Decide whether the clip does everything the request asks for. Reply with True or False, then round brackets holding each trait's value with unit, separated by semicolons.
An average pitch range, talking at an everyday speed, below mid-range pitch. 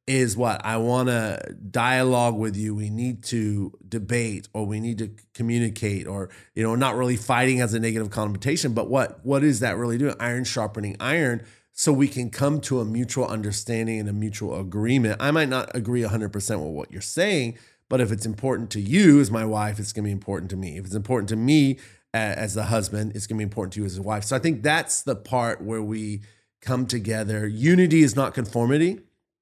False (3.1 semitones; 215 wpm; 115 Hz)